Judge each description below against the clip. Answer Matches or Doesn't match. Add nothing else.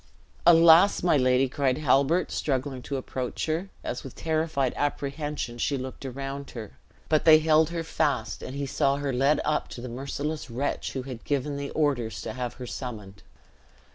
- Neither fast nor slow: Matches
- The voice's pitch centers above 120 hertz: Matches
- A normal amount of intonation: Matches